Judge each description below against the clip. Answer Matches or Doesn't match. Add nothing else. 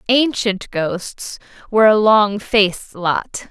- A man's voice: Doesn't match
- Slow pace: Matches